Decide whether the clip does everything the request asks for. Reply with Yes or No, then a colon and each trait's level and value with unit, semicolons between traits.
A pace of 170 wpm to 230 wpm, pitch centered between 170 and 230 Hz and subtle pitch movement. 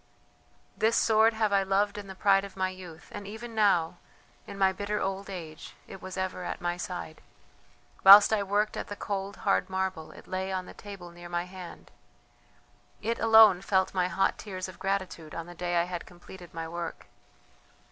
Yes: average, 190 wpm; high, 190 Hz; narrow, 2.3 semitones